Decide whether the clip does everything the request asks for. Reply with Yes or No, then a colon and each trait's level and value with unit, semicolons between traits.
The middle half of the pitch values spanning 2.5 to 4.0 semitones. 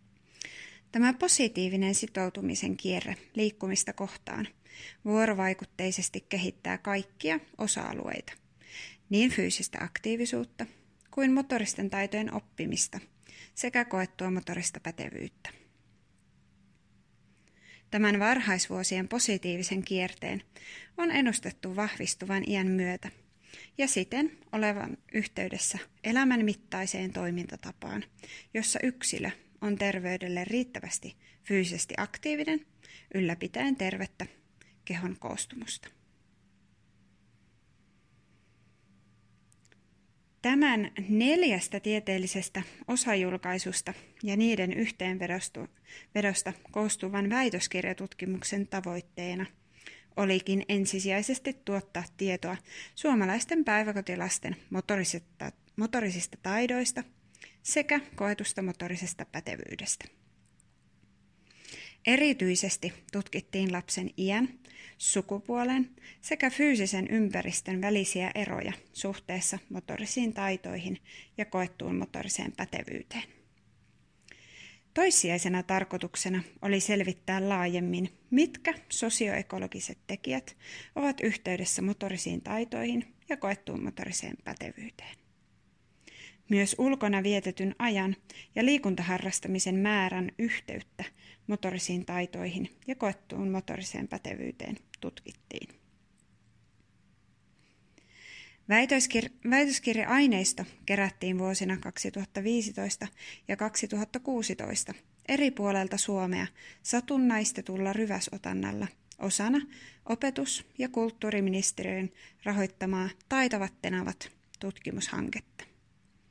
Yes: average, 3.5 semitones